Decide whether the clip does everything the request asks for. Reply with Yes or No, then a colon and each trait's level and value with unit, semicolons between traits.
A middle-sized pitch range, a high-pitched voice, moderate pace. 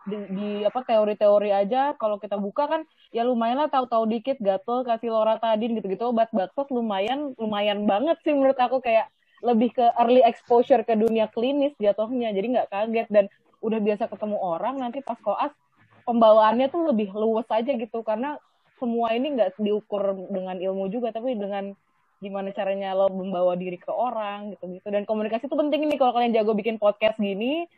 No: average, 3.2 semitones; high, 220 Hz; fast, 175 wpm